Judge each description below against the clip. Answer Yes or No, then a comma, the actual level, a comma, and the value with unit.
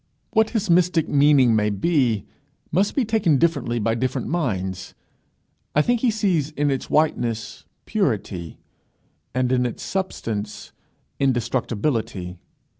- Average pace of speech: No, slow, 120 wpm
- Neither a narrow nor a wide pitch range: No, wide, 7.1 semitones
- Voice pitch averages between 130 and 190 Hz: Yes, low, 135 Hz